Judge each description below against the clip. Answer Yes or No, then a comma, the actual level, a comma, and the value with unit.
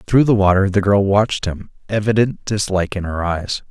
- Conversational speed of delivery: Yes, average, 195 wpm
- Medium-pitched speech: No, low, 100 Hz